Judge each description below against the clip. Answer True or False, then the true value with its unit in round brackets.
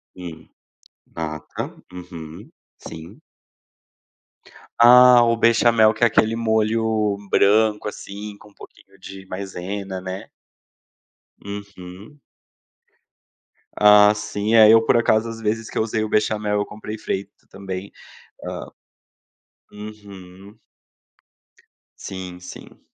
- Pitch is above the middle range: False (105 Hz)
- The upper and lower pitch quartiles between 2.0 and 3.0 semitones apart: True (2.6 semitones)